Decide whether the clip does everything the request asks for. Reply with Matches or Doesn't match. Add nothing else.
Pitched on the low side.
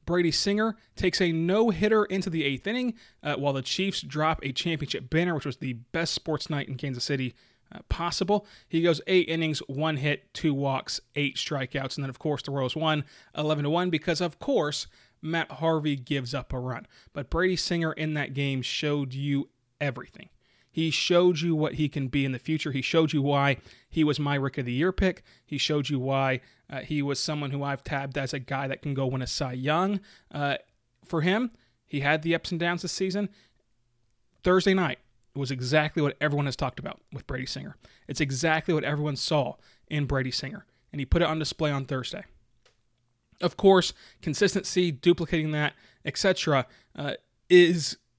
Doesn't match